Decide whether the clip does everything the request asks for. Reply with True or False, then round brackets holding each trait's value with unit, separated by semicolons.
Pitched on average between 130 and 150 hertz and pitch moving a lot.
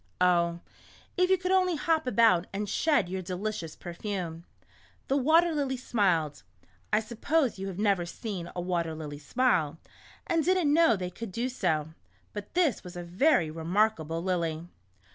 False (195 Hz; 7.5 semitones)